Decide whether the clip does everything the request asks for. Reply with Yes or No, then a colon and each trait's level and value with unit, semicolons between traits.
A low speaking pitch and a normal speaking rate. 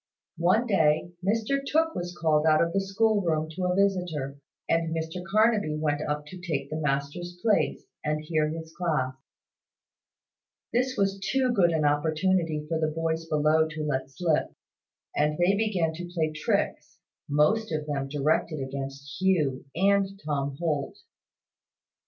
No: medium, 160 Hz; average, 150 wpm